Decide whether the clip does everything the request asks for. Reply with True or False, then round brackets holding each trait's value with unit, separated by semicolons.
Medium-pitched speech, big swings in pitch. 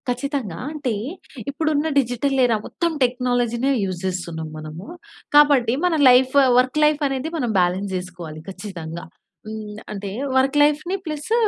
False (245 Hz; 7.2 semitones)